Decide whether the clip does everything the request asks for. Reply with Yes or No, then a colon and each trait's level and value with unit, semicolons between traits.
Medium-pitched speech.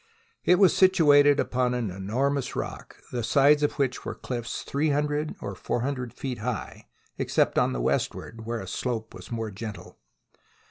No: low, 125 Hz